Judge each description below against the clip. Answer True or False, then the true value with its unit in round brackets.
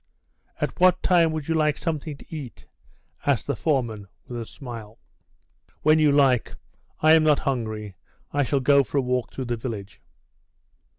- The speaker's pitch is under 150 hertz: True (140 Hz)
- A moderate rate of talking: True (170 wpm)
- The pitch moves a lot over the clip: False (4.5 semitones)